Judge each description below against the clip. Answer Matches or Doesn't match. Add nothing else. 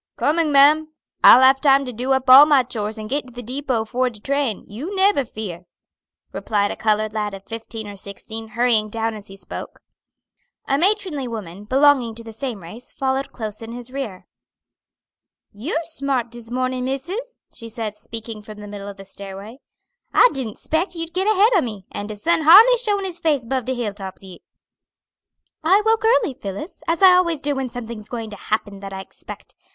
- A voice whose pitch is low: Doesn't match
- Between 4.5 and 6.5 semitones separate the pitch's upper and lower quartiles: Matches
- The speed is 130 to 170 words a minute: Doesn't match